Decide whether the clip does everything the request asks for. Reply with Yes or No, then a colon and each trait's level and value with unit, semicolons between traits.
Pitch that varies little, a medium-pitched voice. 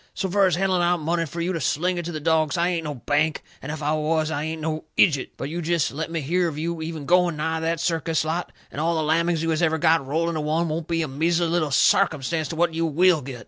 Yes: narrow, 1.7 semitones; medium, 160 Hz